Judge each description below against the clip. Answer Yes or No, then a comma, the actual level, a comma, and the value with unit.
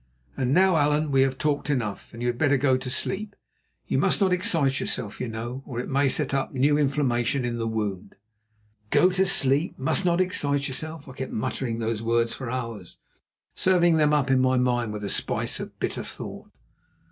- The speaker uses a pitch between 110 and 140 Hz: Yes, low, 135 Hz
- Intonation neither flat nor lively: Yes, average, 3.8 semitones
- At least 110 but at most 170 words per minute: No, average, 200 wpm